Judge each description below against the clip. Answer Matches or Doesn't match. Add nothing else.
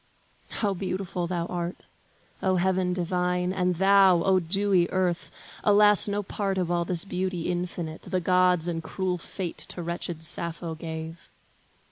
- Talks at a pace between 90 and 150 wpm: Matches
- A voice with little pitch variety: Matches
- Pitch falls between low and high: Matches